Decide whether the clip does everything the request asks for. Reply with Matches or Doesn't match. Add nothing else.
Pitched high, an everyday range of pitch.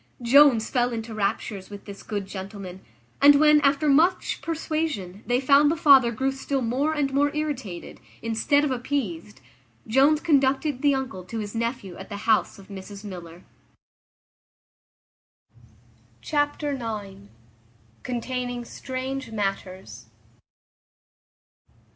Doesn't match